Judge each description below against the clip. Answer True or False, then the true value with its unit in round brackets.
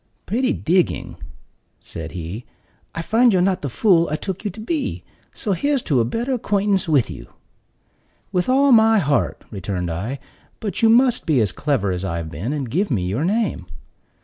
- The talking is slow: False (180 wpm)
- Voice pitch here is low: False (170 Hz)